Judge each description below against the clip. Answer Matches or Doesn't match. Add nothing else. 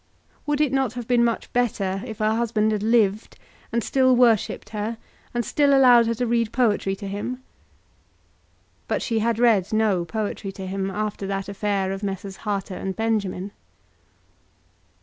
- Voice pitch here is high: Matches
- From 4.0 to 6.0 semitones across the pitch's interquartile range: Doesn't match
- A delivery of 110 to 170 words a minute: Matches